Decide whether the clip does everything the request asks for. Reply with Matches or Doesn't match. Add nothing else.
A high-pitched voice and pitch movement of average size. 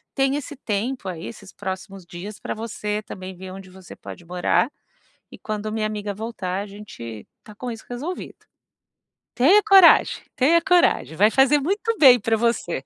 Doesn't match